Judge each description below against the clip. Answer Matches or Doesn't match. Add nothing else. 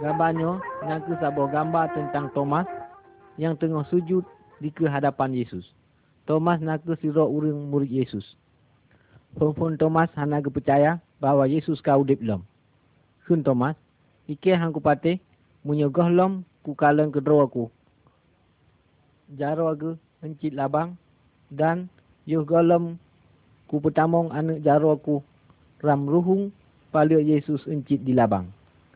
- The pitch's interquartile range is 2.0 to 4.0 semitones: Matches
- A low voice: Doesn't match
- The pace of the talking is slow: Doesn't match